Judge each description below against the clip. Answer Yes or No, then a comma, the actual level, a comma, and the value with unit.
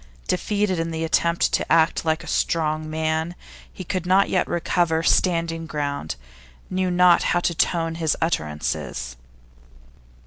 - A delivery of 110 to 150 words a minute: Yes, average, 140 wpm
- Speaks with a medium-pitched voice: Yes, medium, 165 Hz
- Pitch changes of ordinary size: No, narrow, 1.9 semitones